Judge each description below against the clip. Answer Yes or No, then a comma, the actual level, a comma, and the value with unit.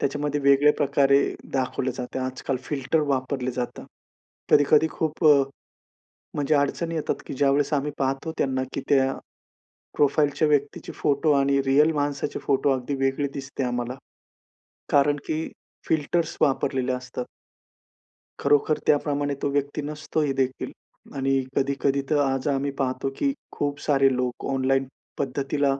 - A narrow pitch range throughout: Yes, narrow, 1.5 semitones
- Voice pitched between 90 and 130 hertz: No, medium, 140 Hz